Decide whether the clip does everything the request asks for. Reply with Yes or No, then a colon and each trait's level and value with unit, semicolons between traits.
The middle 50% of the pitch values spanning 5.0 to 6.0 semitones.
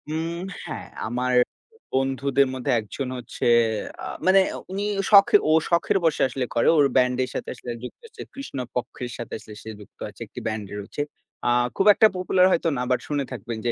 Yes: average, 5.3 semitones